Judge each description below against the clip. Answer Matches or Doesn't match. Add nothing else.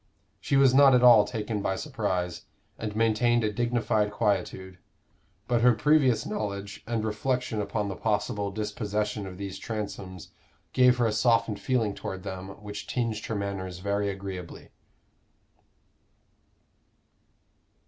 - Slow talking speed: Matches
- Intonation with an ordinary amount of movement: Matches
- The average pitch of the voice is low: Matches